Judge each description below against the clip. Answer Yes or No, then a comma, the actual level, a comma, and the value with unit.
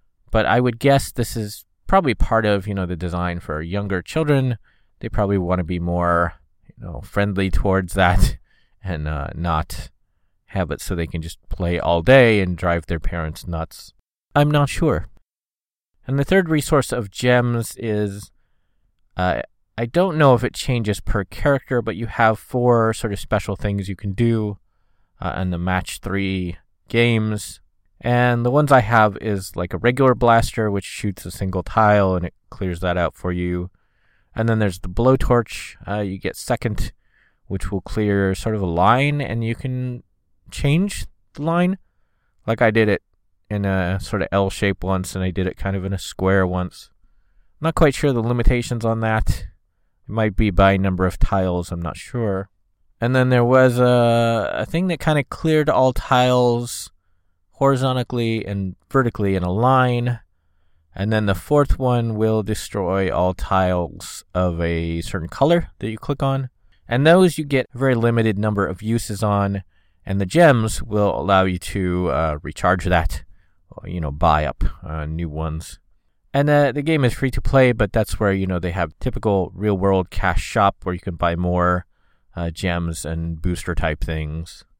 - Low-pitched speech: Yes, low, 100 Hz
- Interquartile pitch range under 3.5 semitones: No, average, 5.1 semitones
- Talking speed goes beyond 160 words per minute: Yes, average, 180 wpm